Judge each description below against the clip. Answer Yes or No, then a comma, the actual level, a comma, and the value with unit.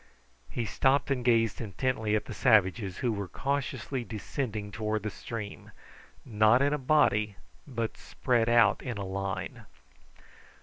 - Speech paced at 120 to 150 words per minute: Yes, average, 140 wpm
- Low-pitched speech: Yes, low, 115 Hz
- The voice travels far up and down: No, average, 3.4 semitones